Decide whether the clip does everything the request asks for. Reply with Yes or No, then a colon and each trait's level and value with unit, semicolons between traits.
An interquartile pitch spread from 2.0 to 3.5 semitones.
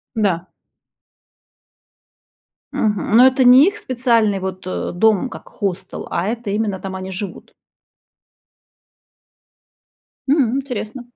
No: average, 4.6 semitones